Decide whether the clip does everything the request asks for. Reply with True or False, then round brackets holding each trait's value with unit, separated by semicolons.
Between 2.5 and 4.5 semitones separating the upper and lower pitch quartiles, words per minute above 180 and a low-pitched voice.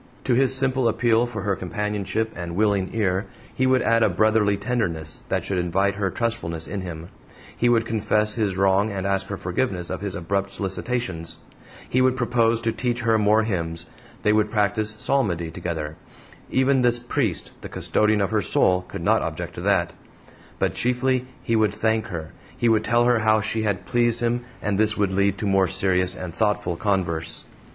True (3.6 semitones; 190 wpm; 105 Hz)